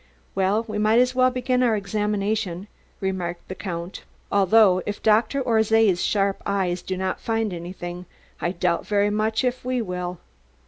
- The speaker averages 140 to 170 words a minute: Yes, average, 155 wpm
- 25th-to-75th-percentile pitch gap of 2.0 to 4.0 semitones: Yes, average, 3.3 semitones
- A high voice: Yes, high, 205 Hz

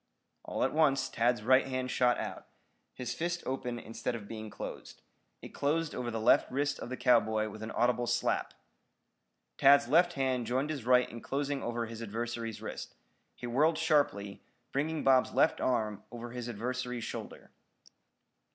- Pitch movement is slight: No, average, 3.1 semitones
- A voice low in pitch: Yes, low, 125 Hz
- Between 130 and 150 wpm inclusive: No, average, 165 wpm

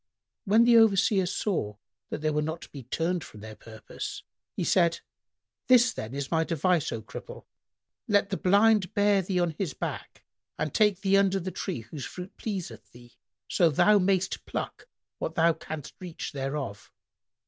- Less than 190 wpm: Yes, average, 170 wpm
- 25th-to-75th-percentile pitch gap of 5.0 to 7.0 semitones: Yes, wide, 5.6 semitones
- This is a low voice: No, medium, 175 Hz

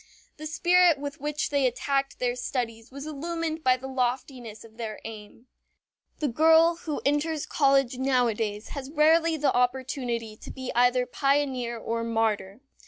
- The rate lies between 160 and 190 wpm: No, average, 150 wpm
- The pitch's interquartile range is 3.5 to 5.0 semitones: Yes, average, 3.9 semitones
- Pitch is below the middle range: No, very high, 265 Hz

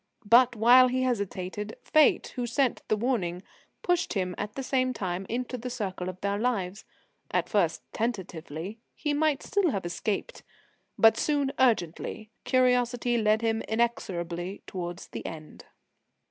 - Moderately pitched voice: No, high, 225 Hz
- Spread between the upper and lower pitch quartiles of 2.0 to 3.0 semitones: No, average, 5.1 semitones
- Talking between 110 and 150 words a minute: Yes, average, 145 wpm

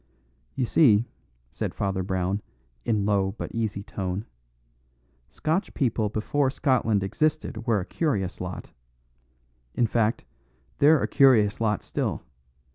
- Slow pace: Yes, slow, 120 wpm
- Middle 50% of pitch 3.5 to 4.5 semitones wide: No, average, 4.9 semitones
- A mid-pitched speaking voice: No, low, 110 Hz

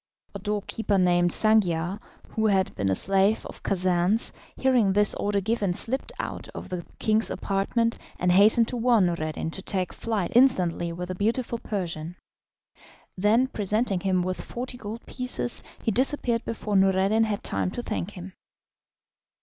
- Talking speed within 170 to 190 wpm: No, average, 155 wpm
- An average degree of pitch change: Yes, average, 3.7 semitones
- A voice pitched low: No, high, 200 Hz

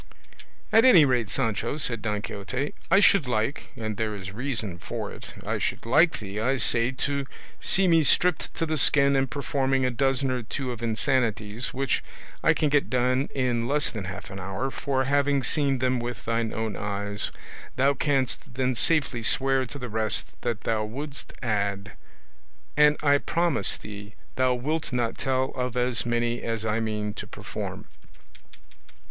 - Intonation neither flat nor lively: Yes, average, 3.9 semitones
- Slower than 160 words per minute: No, average, 175 wpm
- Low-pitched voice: Yes, low, 125 Hz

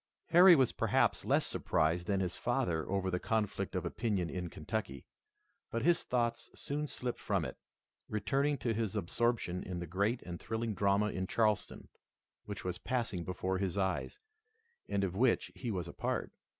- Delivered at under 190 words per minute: Yes, average, 170 wpm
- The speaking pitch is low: Yes, low, 100 Hz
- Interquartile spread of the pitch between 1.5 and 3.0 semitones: No, average, 4.4 semitones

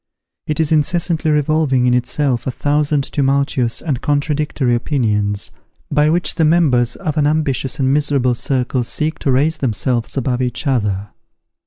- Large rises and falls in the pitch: No, average, 3.4 semitones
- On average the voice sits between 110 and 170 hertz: Yes, medium, 140 Hz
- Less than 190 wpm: Yes, average, 150 wpm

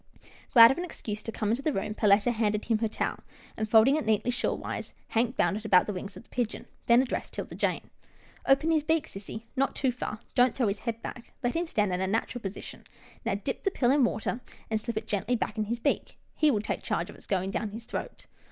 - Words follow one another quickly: Yes, fast, 255 wpm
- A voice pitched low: No, high, 225 Hz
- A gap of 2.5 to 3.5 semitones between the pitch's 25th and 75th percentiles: Yes, average, 3.0 semitones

